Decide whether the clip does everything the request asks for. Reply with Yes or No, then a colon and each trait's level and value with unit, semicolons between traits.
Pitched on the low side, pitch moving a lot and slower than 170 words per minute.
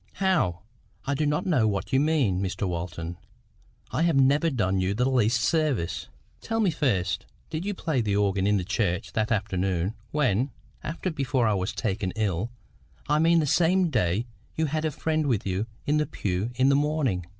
No: low, 120 Hz; wide, 7.8 semitones; average, 175 wpm